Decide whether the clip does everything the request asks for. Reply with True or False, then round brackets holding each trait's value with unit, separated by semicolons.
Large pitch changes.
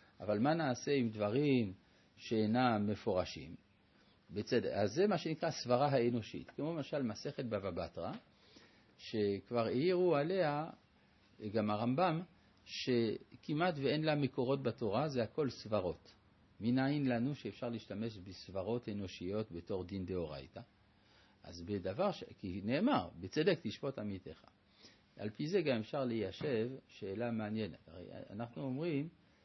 False (5.0 semitones)